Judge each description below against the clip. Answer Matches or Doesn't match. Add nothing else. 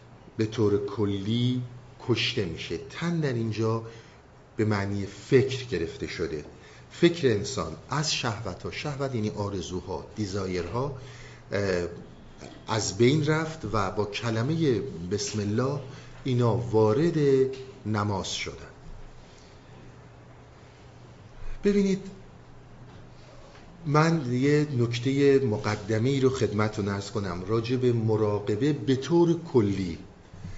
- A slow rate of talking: Matches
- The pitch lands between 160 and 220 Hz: Doesn't match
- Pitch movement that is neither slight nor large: Matches